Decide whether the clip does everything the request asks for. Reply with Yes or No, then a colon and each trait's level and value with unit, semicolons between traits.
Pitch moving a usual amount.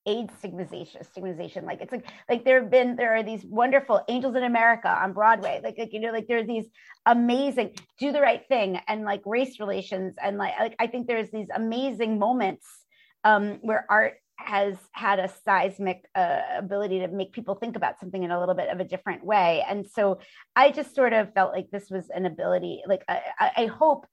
Yes: average, 3.8 semitones